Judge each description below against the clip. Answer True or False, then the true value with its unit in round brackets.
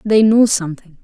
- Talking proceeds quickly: False (175 wpm)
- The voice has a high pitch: True (200 Hz)